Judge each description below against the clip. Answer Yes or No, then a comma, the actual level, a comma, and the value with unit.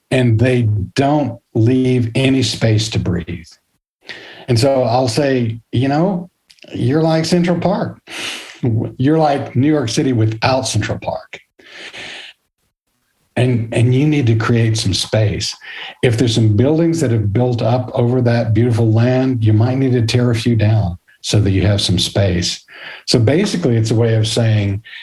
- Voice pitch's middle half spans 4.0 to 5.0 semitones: No, average, 3.0 semitones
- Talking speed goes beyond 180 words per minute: No, average, 160 wpm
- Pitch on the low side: Yes, low, 120 Hz